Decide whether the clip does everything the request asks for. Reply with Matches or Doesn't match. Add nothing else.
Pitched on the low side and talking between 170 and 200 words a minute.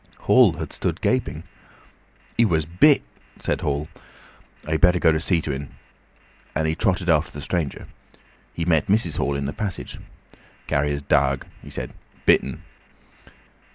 Doesn't match